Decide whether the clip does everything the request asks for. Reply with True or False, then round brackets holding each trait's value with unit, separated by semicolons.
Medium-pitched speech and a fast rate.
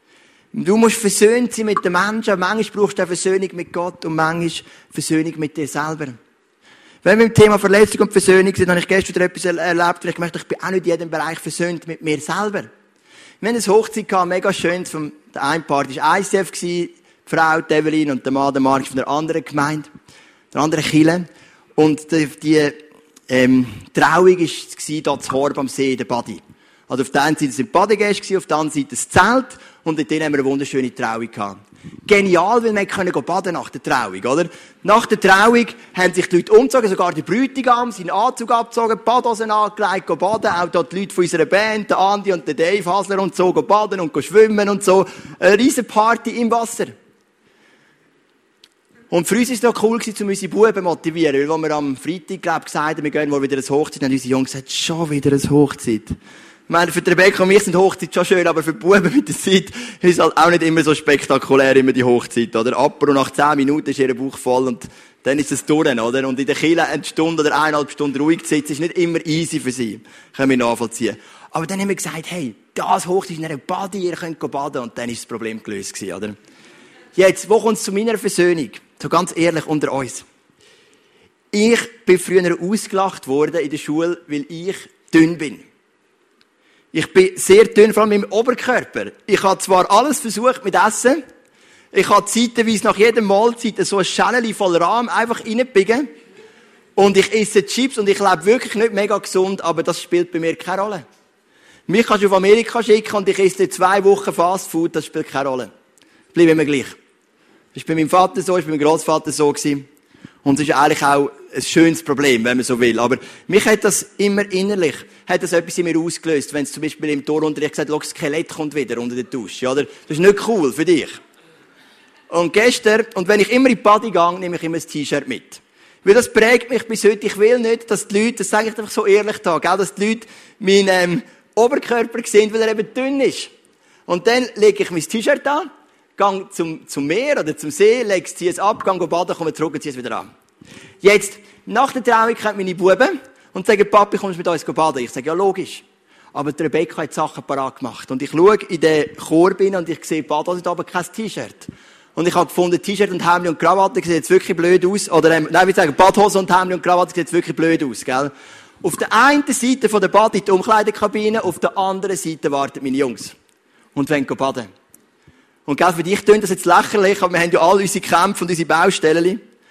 True (180 Hz; 215 wpm)